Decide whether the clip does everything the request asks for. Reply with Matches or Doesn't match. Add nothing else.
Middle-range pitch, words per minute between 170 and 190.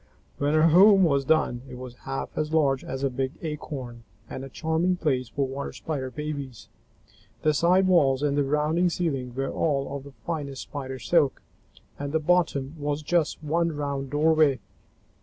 Matches